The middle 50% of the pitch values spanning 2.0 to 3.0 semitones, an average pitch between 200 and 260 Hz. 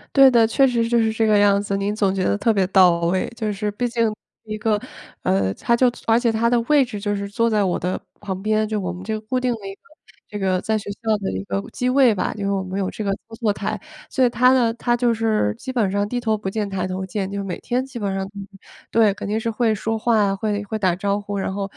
Yes: average, 2.7 semitones; high, 210 Hz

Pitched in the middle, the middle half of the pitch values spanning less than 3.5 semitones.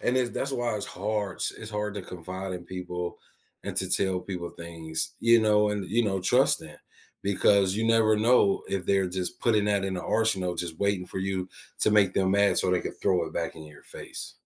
No: very low, 95 Hz; average, 2.8 semitones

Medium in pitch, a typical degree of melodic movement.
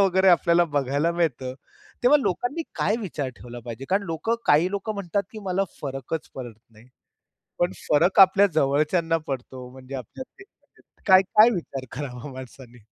No: medium, 160 Hz; wide, 6.4 semitones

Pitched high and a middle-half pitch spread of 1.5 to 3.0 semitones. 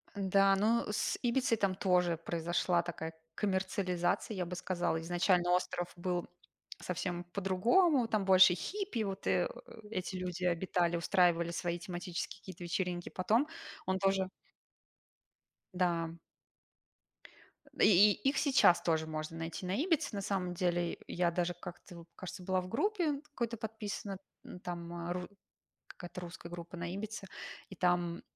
No: medium, 180 Hz; narrow, 2.4 semitones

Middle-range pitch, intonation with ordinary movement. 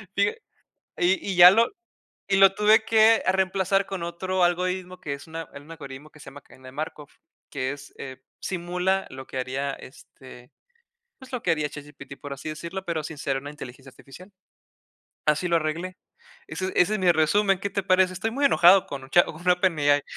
Yes: medium, 170 Hz; average, 4.7 semitones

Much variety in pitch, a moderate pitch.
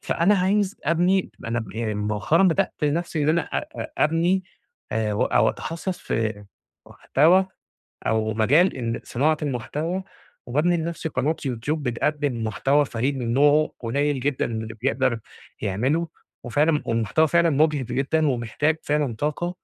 Yes: wide, 5.8 semitones; medium, 145 Hz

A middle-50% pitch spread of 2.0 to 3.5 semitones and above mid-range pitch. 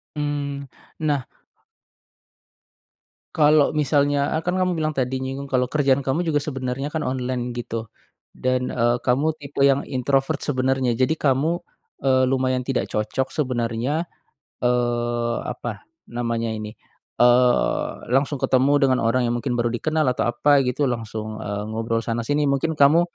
No: average, 3.0 semitones; low, 130 Hz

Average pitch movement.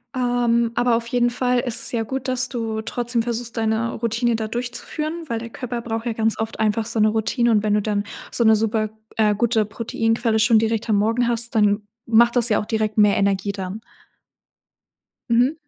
No: narrow, 1.7 semitones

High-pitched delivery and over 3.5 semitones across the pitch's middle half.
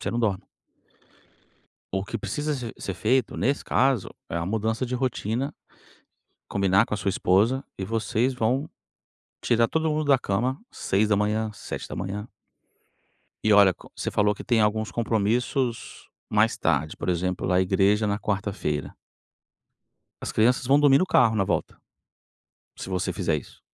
No: low, 110 Hz; average, 4.1 semitones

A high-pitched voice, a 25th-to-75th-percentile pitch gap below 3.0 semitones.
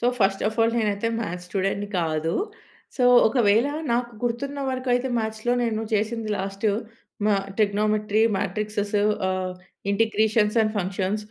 Yes: high, 215 Hz; narrow, 2.4 semitones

